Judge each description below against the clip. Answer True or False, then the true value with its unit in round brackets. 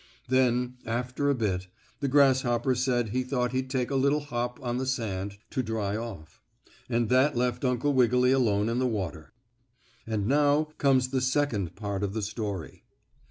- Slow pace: False (170 wpm)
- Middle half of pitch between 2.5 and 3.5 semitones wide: True (3.1 semitones)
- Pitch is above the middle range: False (125 Hz)